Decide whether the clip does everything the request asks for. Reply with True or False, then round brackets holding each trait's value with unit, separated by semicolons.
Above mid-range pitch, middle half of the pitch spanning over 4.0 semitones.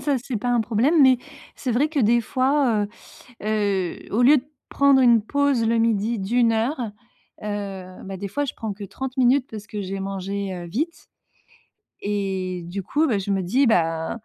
True (220 Hz; 4.7 semitones)